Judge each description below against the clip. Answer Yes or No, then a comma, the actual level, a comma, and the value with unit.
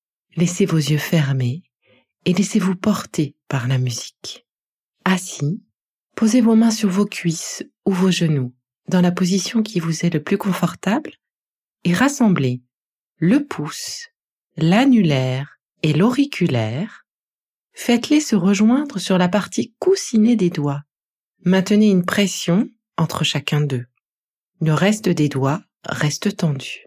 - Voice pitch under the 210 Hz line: Yes, medium, 185 Hz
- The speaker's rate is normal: No, slow, 125 wpm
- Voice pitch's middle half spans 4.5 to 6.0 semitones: Yes, wide, 5.6 semitones